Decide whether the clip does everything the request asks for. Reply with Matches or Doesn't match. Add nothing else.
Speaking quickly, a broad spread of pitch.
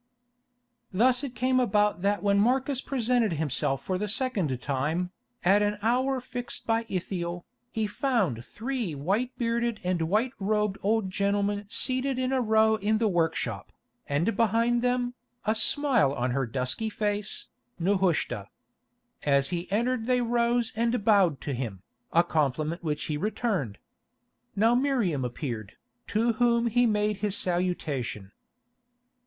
Doesn't match